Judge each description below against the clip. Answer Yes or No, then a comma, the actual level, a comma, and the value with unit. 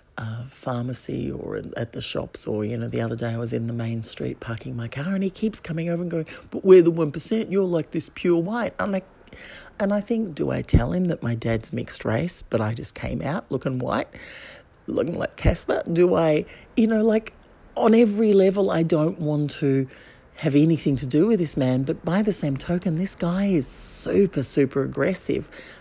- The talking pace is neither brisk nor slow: No, fast, 210 wpm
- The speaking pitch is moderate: Yes, medium, 160 Hz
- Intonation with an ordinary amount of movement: No, wide, 6.7 semitones